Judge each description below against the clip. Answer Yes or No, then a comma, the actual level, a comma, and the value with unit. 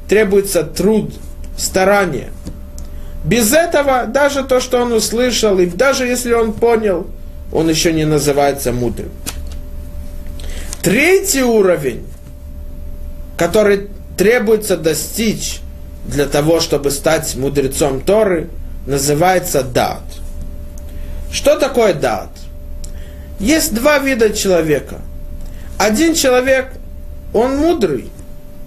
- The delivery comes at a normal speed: No, slow, 90 wpm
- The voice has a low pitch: No, medium, 150 Hz